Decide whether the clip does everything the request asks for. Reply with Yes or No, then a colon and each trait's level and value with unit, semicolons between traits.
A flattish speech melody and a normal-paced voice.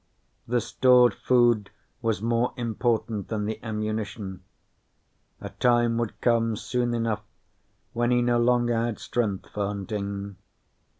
No: narrow, 2.2 semitones; slow, 125 wpm